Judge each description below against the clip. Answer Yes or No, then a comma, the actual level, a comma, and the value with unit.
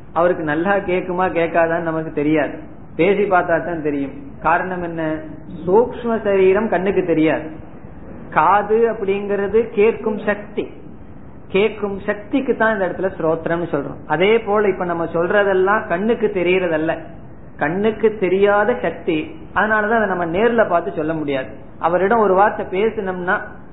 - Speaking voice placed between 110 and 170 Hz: No, medium, 185 Hz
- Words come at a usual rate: Yes, average, 105 wpm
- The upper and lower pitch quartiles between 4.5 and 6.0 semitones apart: No, average, 4.0 semitones